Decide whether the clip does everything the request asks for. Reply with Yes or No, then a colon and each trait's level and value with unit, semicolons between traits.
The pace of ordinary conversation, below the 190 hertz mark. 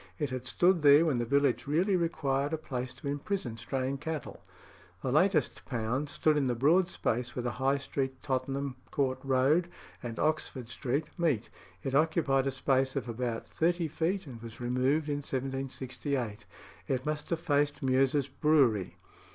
Yes: average, 165 wpm; low, 135 Hz